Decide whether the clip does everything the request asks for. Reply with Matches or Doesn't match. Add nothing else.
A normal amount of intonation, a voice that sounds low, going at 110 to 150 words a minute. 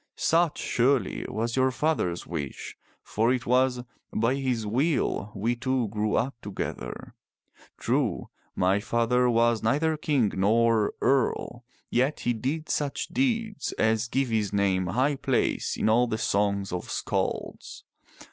Matches